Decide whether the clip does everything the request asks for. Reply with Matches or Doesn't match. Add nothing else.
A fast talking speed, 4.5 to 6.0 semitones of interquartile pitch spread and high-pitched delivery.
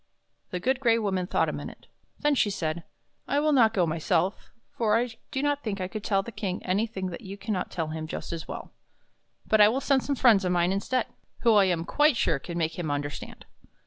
Matches